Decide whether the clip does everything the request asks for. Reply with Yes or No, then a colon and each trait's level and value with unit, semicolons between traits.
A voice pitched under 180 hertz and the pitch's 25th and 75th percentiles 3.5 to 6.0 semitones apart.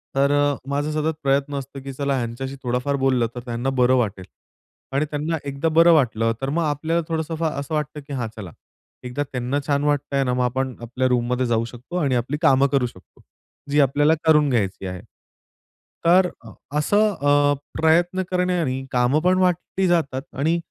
Yes: medium, 140 Hz; average, 3.8 semitones